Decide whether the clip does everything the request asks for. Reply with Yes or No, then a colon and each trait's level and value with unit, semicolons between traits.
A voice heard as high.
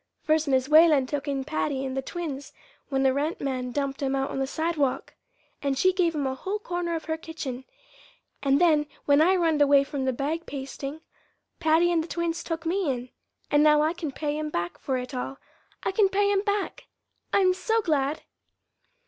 Yes: very high, 300 Hz